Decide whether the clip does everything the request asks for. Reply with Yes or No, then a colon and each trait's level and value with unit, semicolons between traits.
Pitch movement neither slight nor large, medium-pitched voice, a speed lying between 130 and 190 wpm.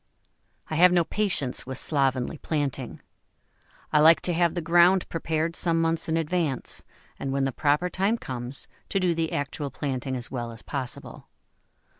Yes: average, 4.1 semitones; medium, 155 Hz; average, 165 wpm